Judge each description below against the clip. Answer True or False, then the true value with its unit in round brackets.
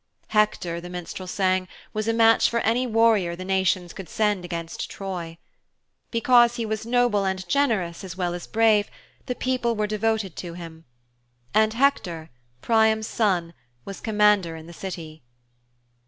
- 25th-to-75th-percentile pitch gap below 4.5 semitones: True (4.1 semitones)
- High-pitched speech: True (200 Hz)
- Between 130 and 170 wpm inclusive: True (155 wpm)